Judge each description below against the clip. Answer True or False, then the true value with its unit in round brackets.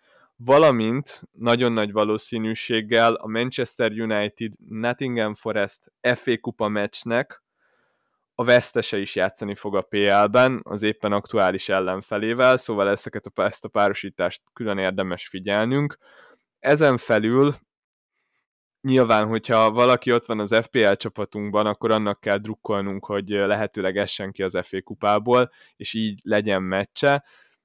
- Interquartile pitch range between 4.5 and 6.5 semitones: False (2.7 semitones)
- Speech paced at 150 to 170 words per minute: False (125 wpm)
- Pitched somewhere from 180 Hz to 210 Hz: False (110 Hz)